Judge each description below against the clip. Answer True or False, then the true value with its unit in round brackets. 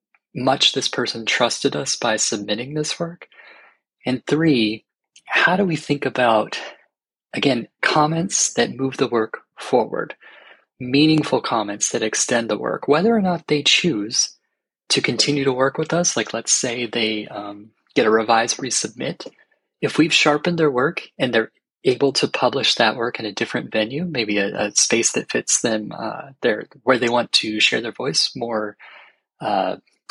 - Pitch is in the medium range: False (125 Hz)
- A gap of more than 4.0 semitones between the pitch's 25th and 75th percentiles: True (5.4 semitones)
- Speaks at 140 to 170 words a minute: True (165 wpm)